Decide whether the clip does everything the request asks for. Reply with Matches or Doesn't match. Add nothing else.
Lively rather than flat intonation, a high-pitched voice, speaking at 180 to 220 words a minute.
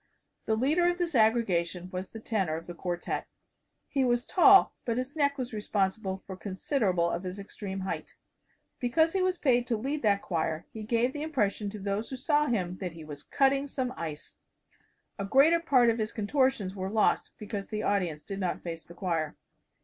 Matches